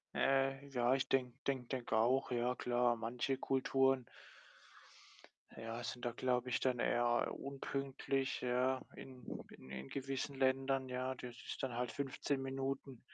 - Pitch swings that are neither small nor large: No, narrow, 1.6 semitones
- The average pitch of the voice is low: Yes, low, 130 Hz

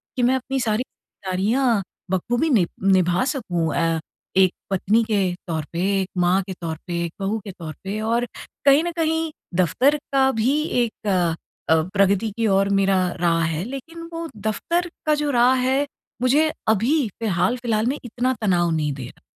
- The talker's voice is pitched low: No, high, 220 Hz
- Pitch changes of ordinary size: No, wide, 6.2 semitones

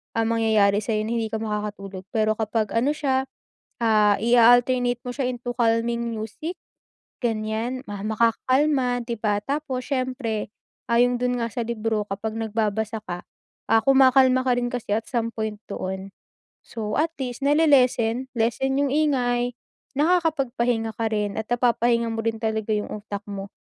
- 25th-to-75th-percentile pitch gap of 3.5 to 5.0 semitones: No, average, 2.7 semitones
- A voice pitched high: Yes, high, 230 Hz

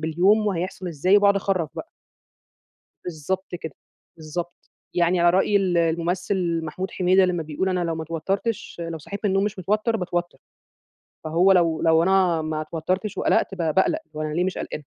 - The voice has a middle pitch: Yes, medium, 180 Hz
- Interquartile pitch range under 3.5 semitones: Yes, average, 2.8 semitones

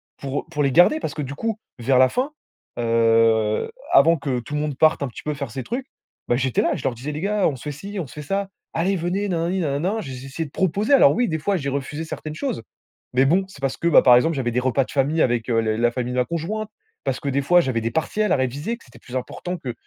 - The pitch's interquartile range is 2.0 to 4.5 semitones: No, wide, 5.6 semitones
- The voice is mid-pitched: Yes, medium, 145 Hz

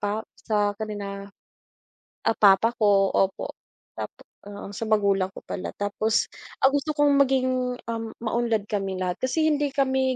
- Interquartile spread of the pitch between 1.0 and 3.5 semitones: No, average, 4.3 semitones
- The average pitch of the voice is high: Yes, high, 220 Hz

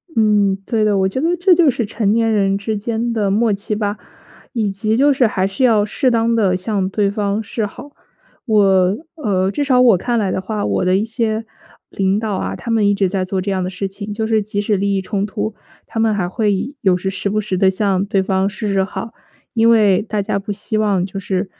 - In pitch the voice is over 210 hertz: No, high, 205 Hz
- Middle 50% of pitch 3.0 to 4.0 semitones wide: No, narrow, 2.4 semitones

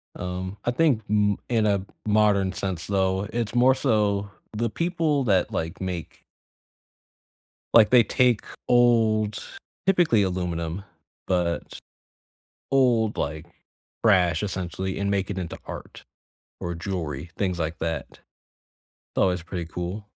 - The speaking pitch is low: Yes, low, 100 Hz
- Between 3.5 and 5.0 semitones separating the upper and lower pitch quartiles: Yes, average, 3.9 semitones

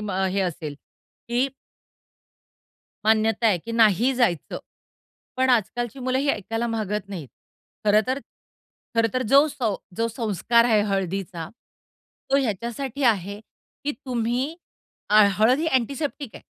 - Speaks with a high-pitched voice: Yes, high, 230 Hz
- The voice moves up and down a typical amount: Yes, average, 4.1 semitones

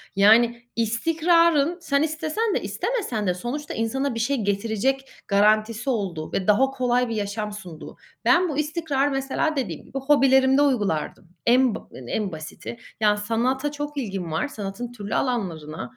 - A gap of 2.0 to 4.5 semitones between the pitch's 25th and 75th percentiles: No, average, 5.3 semitones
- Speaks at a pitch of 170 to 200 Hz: No, high, 240 Hz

